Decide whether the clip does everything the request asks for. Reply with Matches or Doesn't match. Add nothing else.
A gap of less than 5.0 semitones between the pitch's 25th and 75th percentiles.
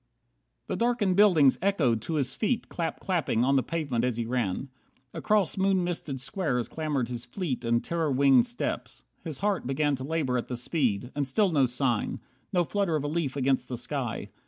Doesn't match